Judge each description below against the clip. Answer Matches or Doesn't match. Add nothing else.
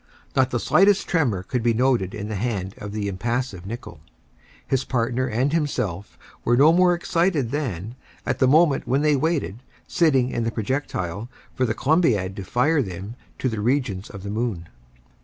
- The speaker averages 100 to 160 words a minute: Doesn't match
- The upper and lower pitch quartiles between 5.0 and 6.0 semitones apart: Matches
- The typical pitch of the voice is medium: Doesn't match